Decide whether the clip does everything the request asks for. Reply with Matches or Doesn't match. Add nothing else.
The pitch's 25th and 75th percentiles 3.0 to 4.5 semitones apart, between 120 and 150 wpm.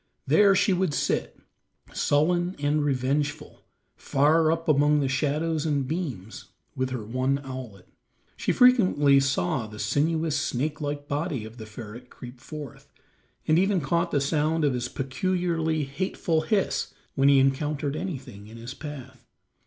Matches